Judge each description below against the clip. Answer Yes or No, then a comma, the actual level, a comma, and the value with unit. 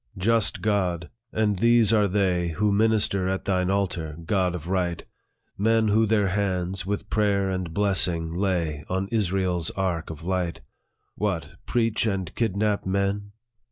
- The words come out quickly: No, average, 155 wpm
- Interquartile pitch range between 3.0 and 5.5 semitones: No, narrow, 2.6 semitones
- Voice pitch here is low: Yes, very low, 95 Hz